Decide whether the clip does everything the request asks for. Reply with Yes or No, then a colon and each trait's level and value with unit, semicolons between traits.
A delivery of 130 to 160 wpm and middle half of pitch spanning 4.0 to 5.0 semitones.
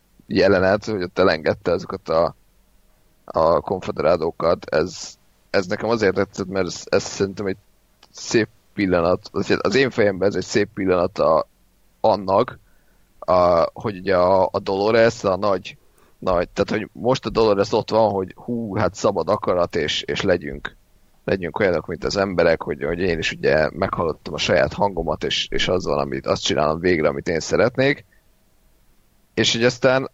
No: fast, 155 wpm; average, 3.2 semitones